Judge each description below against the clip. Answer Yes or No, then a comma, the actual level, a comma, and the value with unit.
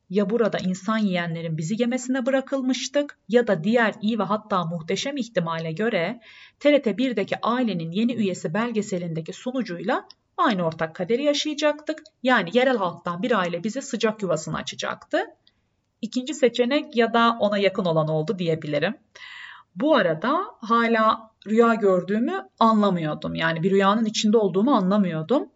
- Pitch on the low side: No, high, 220 Hz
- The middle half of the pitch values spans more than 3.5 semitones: Yes, average, 5.3 semitones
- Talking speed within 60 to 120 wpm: No, average, 135 wpm